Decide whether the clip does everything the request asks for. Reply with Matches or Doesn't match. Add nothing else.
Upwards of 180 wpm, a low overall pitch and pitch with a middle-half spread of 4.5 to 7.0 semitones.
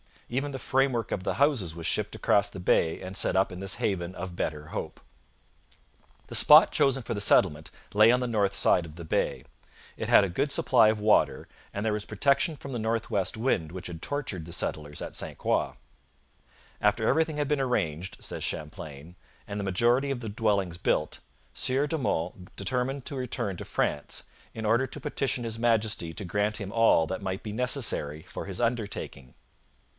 Matches